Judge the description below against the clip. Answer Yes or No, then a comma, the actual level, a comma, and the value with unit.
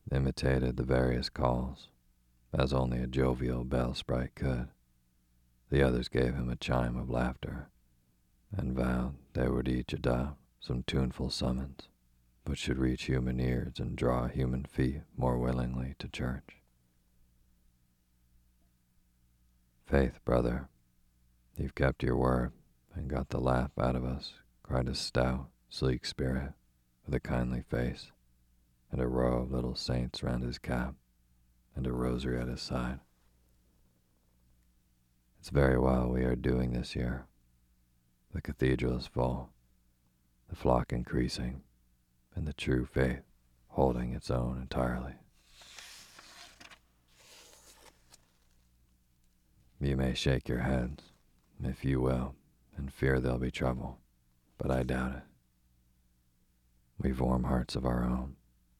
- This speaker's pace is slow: Yes, slow, 125 wpm